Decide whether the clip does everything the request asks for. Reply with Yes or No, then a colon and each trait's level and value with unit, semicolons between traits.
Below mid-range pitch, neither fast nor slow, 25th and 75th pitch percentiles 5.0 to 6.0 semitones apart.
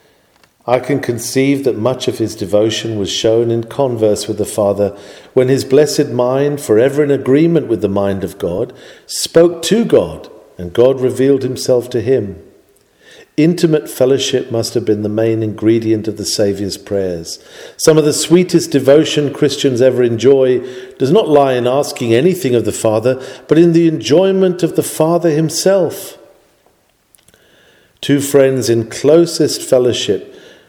Yes: low, 130 Hz; average, 155 wpm; average, 5.3 semitones